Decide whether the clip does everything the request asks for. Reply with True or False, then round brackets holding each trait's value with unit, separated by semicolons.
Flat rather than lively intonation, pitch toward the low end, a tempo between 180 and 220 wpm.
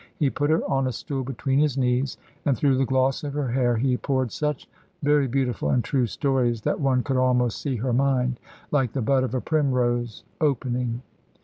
True (2.0 semitones; 130 Hz; 200 wpm)